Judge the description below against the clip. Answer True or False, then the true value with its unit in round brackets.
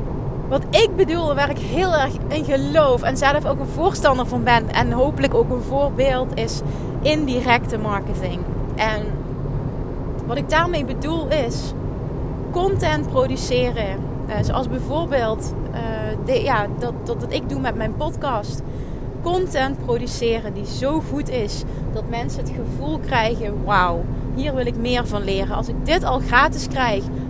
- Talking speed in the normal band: True (150 wpm)